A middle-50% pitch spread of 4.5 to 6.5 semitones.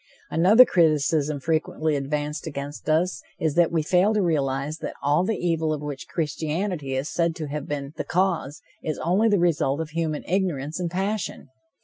No: average, 3.1 semitones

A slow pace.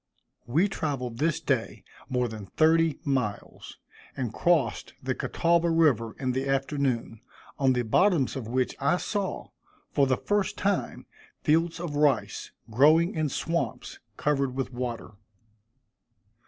Yes: slow, 130 wpm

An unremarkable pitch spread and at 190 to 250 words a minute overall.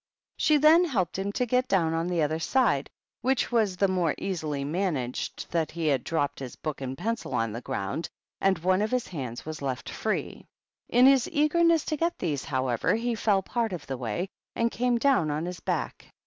No: wide, 8.4 semitones; fast, 205 wpm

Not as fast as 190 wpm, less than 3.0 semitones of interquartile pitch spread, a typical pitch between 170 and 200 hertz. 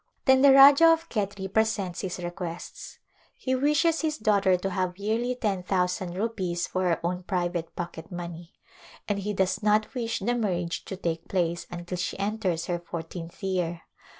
No: average, 170 wpm; average, 3.9 semitones; high, 190 Hz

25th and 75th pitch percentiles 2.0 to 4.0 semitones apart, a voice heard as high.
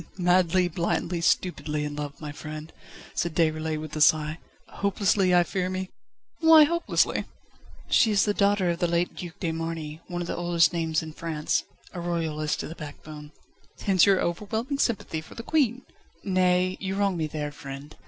No: average, 3.3 semitones; medium, 170 Hz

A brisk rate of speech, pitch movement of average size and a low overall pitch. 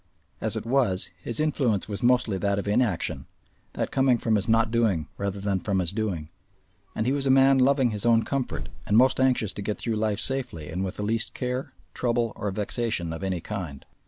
Yes: fast, 210 wpm; average, 4.2 semitones; low, 110 Hz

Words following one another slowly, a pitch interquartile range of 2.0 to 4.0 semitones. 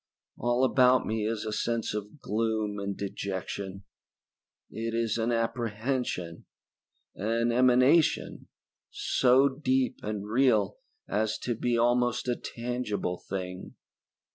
Yes: slow, 115 wpm; average, 2.9 semitones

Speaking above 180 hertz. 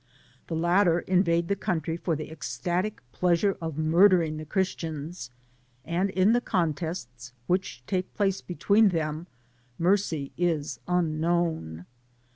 No: medium, 170 Hz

